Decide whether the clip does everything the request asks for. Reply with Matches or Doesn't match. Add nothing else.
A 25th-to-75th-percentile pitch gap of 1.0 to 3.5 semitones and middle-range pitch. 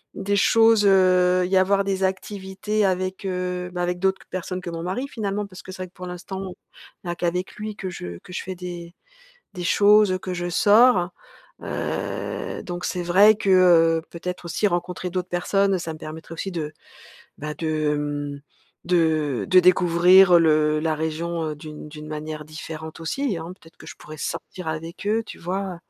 Matches